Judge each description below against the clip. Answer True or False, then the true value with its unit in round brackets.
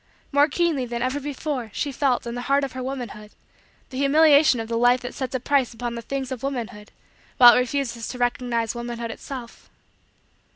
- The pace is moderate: True (195 wpm)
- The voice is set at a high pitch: True (250 Hz)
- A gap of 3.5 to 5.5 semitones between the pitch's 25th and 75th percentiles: False (2.6 semitones)